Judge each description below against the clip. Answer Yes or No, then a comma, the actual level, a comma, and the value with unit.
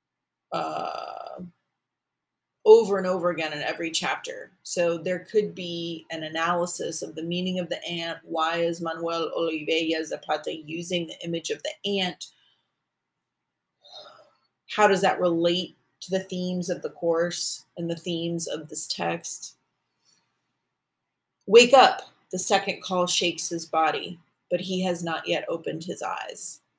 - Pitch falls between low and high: Yes, medium, 175 Hz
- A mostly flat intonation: Yes, narrow, 1.9 semitones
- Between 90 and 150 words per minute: Yes, average, 140 wpm